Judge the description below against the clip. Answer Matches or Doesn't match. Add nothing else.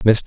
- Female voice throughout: Doesn't match